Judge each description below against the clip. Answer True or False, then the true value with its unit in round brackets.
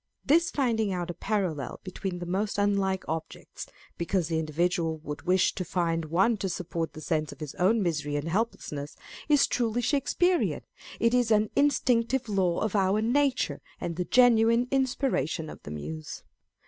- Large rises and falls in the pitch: True (5.9 semitones)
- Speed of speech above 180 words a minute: False (170 wpm)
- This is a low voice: False (190 Hz)